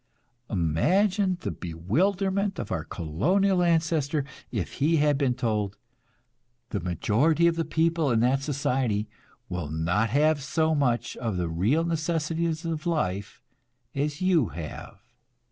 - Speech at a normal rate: No, slow, 130 wpm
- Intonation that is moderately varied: No, wide, 8.2 semitones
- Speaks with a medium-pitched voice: Yes, medium, 145 Hz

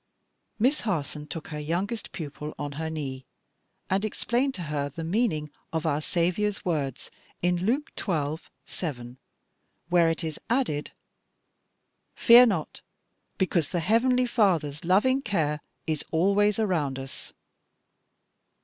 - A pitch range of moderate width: No, wide, 5.7 semitones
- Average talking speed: No, slow, 125 wpm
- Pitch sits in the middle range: Yes, medium, 170 Hz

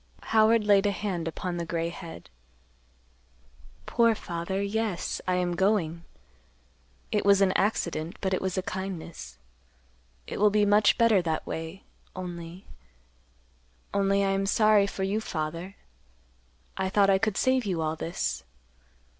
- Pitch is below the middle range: No, high, 190 Hz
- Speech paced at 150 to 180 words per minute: No, average, 140 wpm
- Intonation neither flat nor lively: Yes, average, 3.4 semitones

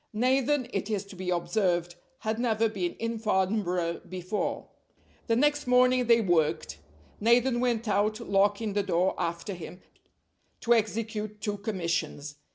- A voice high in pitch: Yes, high, 210 Hz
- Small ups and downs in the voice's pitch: No, average, 4.2 semitones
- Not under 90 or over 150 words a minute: Yes, average, 140 wpm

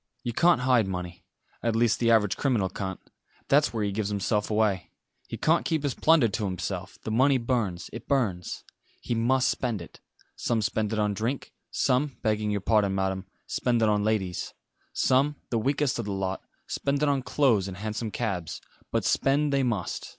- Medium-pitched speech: No, low, 110 Hz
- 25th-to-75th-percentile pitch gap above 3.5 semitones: Yes, average, 4.7 semitones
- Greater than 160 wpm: Yes, average, 185 wpm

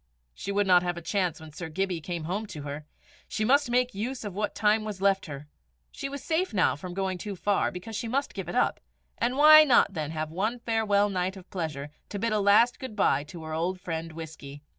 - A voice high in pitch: Yes, high, 195 Hz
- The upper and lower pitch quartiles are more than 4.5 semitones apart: Yes, average, 5.0 semitones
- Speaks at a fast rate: Yes, fast, 235 wpm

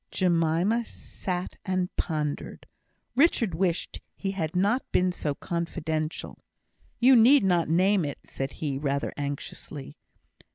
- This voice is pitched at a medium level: Yes, medium, 175 Hz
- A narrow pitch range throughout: No, average, 4.0 semitones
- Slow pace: Yes, slow, 120 wpm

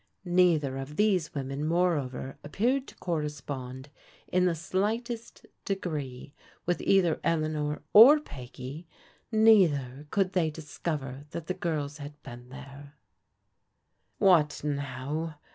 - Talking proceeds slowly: Yes, slow, 110 wpm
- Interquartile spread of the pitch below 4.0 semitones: No, average, 4.4 semitones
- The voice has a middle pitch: Yes, medium, 150 Hz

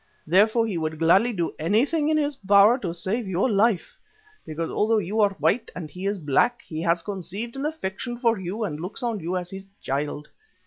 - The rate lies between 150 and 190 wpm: No, fast, 205 wpm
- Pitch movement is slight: No, average, 5.2 semitones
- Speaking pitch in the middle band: No, high, 200 Hz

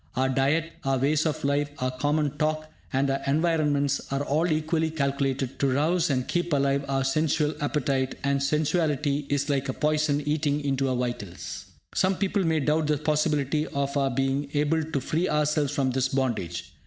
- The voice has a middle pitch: Yes, medium, 145 Hz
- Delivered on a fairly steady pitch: Yes, narrow, 2.2 semitones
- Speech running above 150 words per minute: Yes, average, 180 wpm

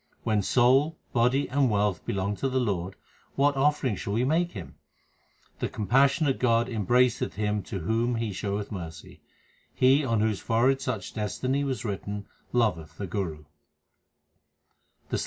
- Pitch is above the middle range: No, low, 115 Hz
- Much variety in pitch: No, average, 4.5 semitones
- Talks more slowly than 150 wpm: Yes, average, 140 wpm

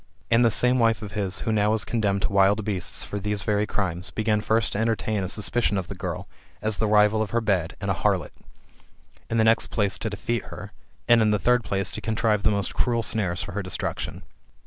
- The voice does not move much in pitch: Yes, narrow, 2.0 semitones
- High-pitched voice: No, low, 105 Hz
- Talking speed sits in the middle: No, fast, 230 wpm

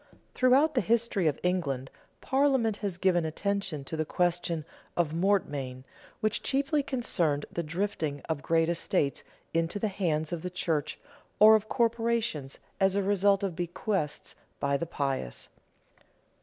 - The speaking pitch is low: No, medium, 180 Hz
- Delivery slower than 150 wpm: Yes, average, 140 wpm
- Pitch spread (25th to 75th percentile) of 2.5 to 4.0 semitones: No, wide, 5.4 semitones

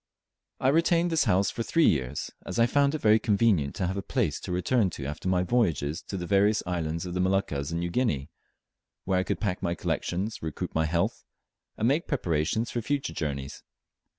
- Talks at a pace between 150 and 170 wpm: No, fast, 205 wpm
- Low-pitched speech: Yes, very low, 95 Hz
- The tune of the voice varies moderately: No, wide, 6.0 semitones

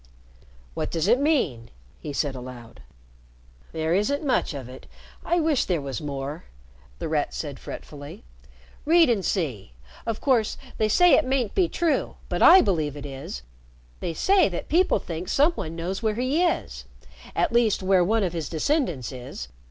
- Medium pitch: Yes, medium, 180 Hz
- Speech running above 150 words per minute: Yes, average, 170 wpm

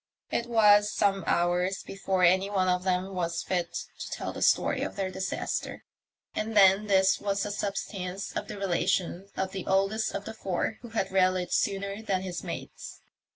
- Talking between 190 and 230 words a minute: No, average, 180 wpm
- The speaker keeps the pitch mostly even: Yes, narrow, 1.7 semitones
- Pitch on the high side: Yes, high, 195 Hz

